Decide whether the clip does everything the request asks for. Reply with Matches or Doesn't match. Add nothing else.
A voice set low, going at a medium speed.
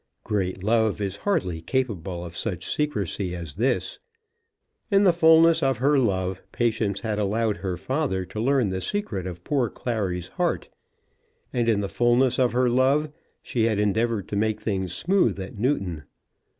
Matches